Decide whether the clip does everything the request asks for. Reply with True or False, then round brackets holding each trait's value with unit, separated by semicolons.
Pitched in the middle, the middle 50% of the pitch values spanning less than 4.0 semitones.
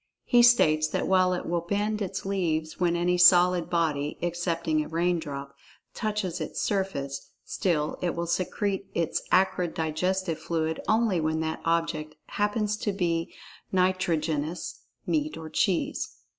True (170 Hz; 3.0 semitones)